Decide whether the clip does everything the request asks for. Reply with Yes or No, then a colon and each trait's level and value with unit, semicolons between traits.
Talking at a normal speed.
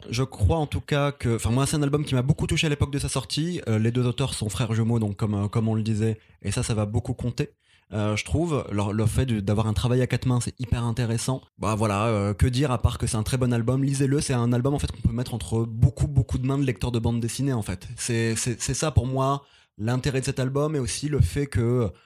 No: fast, 285 wpm